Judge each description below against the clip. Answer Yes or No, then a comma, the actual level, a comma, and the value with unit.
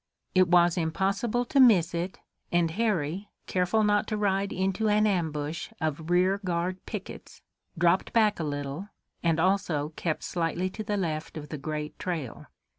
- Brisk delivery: No, average, 160 wpm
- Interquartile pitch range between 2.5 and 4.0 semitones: Yes, average, 3.7 semitones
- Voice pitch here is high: No, medium, 180 Hz